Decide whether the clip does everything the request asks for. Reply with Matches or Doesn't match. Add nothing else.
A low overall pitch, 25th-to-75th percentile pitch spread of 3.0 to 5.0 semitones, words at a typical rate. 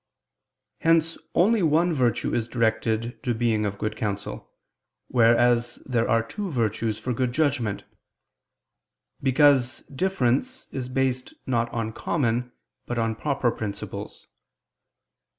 Doesn't match